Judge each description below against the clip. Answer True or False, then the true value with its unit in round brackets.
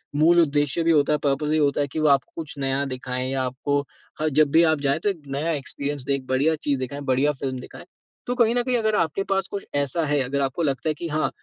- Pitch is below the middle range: False (145 Hz)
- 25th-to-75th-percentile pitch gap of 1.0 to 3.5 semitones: True (2.9 semitones)